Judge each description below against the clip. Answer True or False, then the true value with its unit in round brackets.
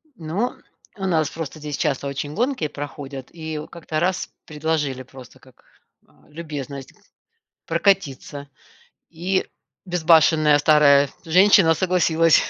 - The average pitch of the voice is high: False (155 Hz)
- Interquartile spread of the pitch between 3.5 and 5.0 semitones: False (2.9 semitones)